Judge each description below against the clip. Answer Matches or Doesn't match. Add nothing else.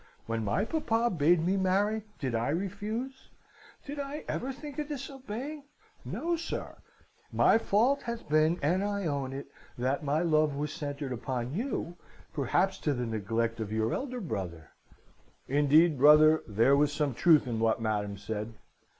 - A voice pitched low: Doesn't match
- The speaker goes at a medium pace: Matches